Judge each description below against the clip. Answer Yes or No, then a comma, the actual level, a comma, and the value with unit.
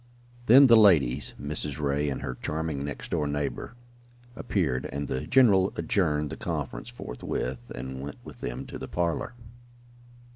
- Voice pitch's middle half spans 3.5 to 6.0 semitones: Yes, wide, 5.5 semitones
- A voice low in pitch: Yes, very low, 75 Hz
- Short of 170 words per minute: Yes, average, 150 wpm